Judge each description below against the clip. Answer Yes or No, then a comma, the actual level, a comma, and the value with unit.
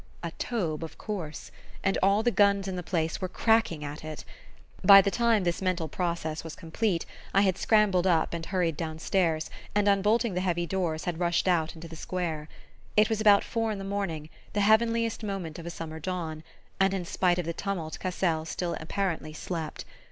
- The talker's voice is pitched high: No, medium, 180 Hz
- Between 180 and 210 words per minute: Yes, average, 195 wpm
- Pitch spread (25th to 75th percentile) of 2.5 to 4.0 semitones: Yes, average, 3.5 semitones